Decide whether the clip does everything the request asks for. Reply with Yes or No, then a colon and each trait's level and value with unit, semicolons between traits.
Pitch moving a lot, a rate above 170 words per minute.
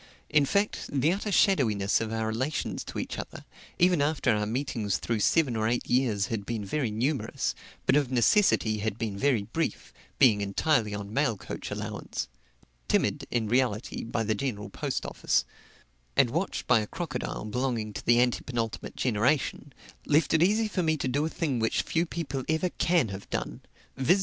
Yes: wide, 5.7 semitones; average, 180 wpm